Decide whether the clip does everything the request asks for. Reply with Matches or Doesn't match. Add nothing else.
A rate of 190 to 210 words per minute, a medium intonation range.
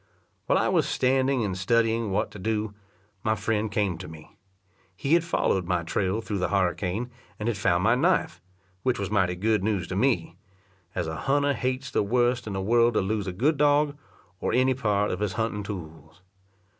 Matches